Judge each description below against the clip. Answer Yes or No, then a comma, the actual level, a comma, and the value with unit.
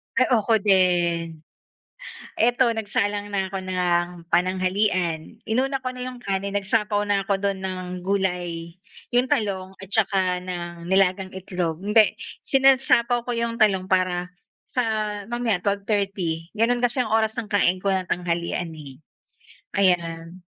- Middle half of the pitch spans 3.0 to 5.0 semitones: Yes, average, 3.6 semitones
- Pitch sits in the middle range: No, high, 195 Hz